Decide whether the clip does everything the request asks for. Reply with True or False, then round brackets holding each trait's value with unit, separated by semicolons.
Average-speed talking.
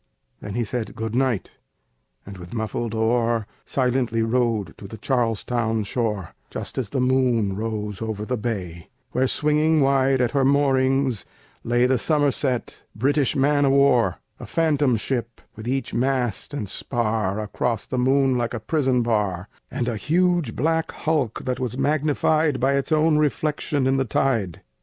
True (160 wpm)